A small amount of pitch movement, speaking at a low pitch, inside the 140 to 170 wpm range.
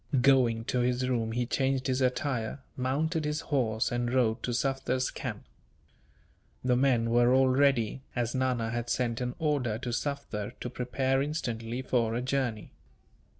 Yes: narrow, 2.1 semitones; low, 125 Hz; average, 155 wpm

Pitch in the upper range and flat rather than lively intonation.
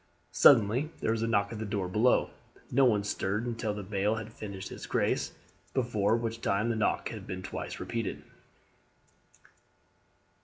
No: low, 110 Hz; narrow, 2.3 semitones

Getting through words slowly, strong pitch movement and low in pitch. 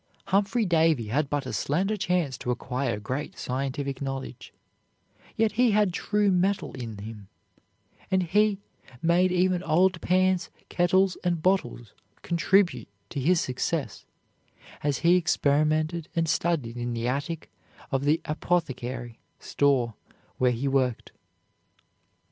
No: slow, 125 wpm; wide, 5.9 semitones; medium, 155 Hz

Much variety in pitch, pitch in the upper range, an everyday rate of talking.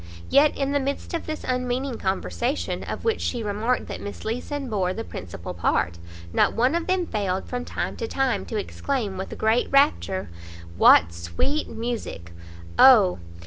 Yes: wide, 6.5 semitones; high, 235 Hz; average, 170 wpm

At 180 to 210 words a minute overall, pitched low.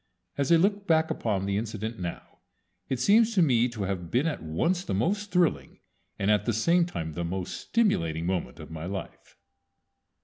Yes: average, 190 wpm; low, 115 Hz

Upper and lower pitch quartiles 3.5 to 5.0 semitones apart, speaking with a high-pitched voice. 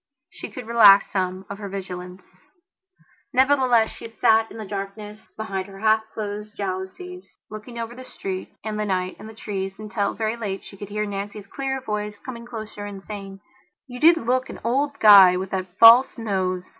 No: average, 2.8 semitones; high, 210 Hz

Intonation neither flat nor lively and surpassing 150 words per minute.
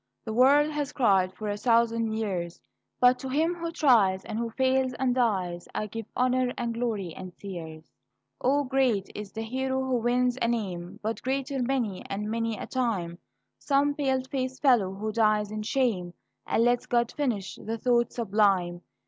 Yes: average, 4.2 semitones; average, 175 wpm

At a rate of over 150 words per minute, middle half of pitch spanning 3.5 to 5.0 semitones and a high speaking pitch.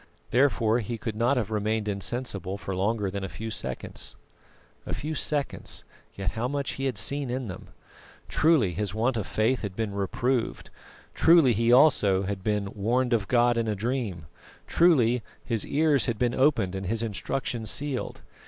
No: average, 170 wpm; average, 4.2 semitones; low, 115 Hz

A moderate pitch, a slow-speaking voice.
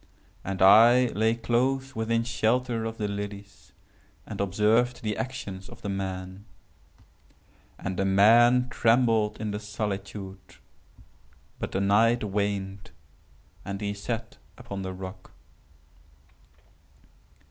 No: low, 105 Hz; slow, 110 wpm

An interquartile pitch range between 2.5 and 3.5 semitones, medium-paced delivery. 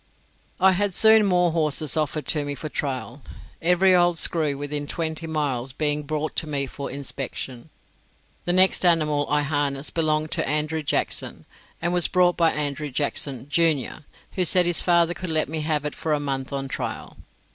Yes: average, 2.9 semitones; average, 180 wpm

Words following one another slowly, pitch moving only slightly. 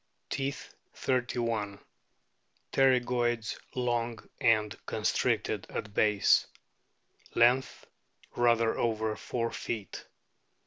Yes: slow, 80 wpm; narrow, 2.1 semitones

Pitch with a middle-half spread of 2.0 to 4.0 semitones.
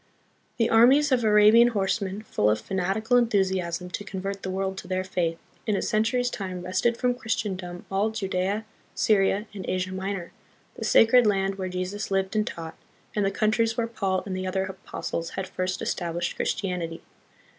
Yes: average, 2.8 semitones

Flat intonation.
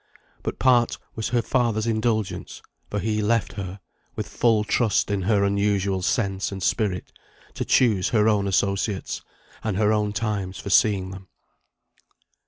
Yes: narrow, 2.1 semitones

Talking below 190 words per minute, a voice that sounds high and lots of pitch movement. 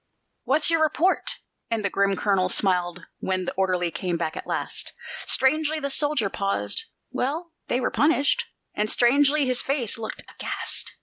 Yes: average, 160 wpm; high, 240 Hz; wide, 7.5 semitones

